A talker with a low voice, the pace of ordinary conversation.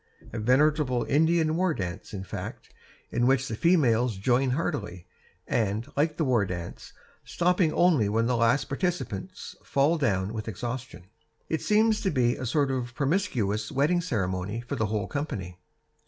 Yes: low, 125 Hz; average, 155 wpm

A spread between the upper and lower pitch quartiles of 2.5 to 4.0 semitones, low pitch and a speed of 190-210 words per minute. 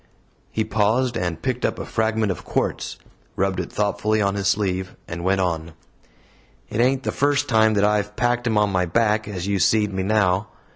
Yes: average, 2.8 semitones; low, 105 Hz; average, 195 wpm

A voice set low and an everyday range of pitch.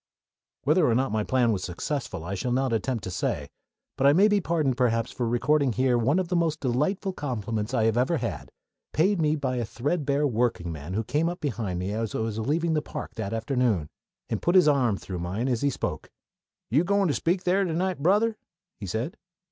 No: low, 130 Hz; wide, 6.3 semitones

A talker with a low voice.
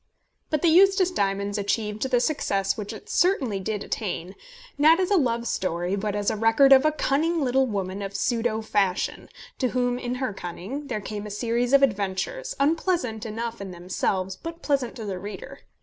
No: high, 230 Hz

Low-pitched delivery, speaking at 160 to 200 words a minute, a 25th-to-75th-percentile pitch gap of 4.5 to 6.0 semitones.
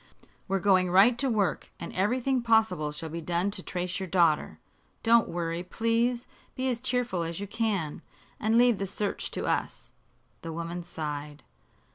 No: high, 190 Hz; average, 165 wpm; average, 5.3 semitones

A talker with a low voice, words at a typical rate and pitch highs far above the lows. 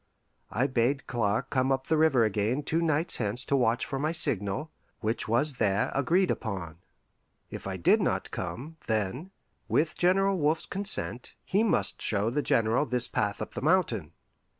Yes: low, 130 Hz; average, 170 wpm; wide, 6.3 semitones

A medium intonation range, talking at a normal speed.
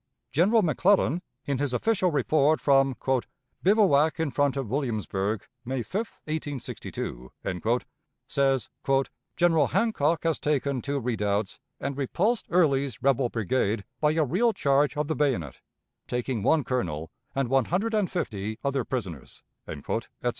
No: average, 4.7 semitones; slow, 130 wpm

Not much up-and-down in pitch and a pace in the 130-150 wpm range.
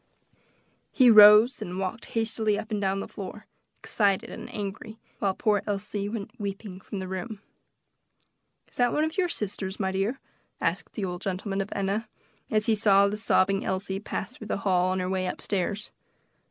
No: narrow, 2.1 semitones; average, 180 wpm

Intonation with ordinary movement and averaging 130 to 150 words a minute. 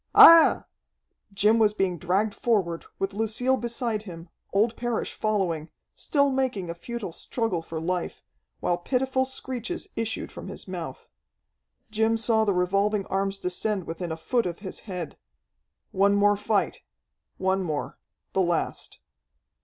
Yes: average, 4.0 semitones; average, 140 wpm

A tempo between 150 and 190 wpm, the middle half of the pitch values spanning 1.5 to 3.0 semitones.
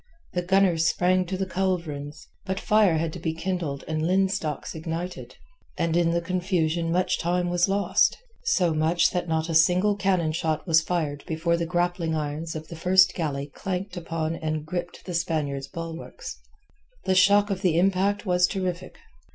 Yes: average, 165 wpm; narrow, 2.5 semitones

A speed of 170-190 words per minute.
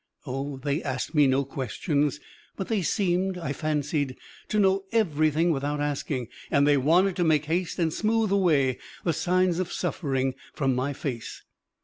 No: average, 160 wpm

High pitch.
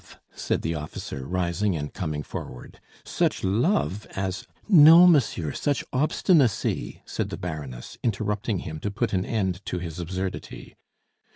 No: very low, 95 Hz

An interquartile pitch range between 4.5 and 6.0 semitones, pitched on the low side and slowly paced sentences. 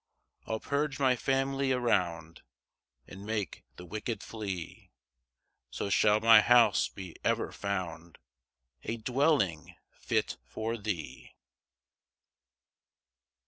Yes: average, 5.3 semitones; low, 110 Hz; slow, 100 wpm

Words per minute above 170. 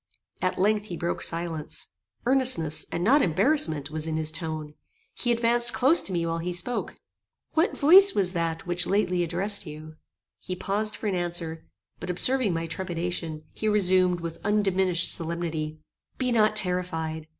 No: average, 160 wpm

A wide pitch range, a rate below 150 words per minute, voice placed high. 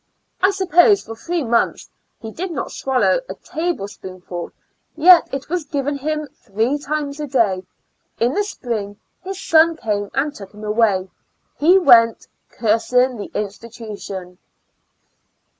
Yes: wide, 7.0 semitones; average, 140 wpm; very high, 255 Hz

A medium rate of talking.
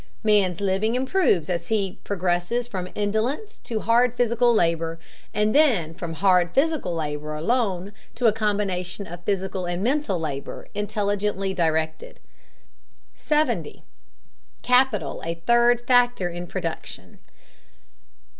No: slow, 115 wpm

